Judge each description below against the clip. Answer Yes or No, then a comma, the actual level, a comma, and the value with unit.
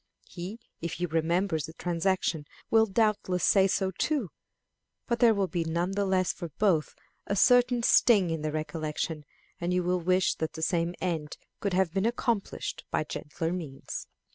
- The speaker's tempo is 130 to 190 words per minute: Yes, average, 170 wpm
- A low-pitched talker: No, medium, 180 Hz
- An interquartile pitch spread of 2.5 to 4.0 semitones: Yes, average, 3.5 semitones